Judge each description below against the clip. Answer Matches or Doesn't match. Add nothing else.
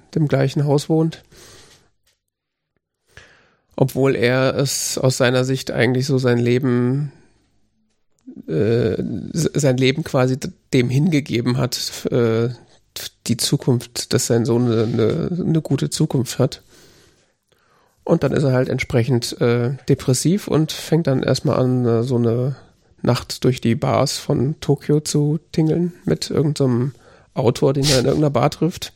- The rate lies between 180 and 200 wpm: Doesn't match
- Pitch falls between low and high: Doesn't match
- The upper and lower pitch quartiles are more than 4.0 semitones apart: Doesn't match